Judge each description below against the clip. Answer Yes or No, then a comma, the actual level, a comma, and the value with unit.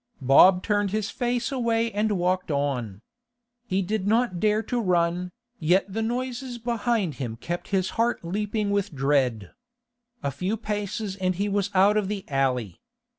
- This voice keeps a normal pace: Yes, average, 160 wpm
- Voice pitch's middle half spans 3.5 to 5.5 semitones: Yes, average, 4.3 semitones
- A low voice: No, high, 195 Hz